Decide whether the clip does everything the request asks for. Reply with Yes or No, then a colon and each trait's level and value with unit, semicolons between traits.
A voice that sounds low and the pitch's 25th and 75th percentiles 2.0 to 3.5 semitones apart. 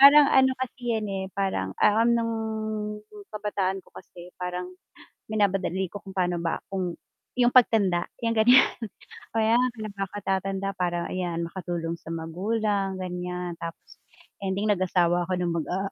No: high, 190 Hz; average, 3.1 semitones